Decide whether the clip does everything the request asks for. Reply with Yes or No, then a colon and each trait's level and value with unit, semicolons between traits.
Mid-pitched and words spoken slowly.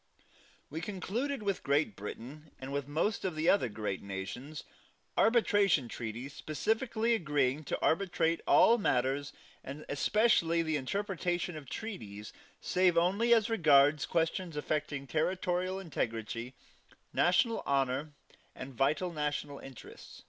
Yes: medium, 155 Hz; slow, 120 wpm